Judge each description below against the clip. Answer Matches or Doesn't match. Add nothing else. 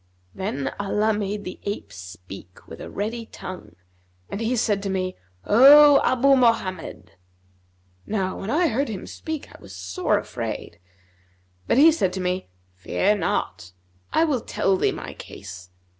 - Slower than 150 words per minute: Doesn't match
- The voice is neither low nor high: Doesn't match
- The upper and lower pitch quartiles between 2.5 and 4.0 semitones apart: Doesn't match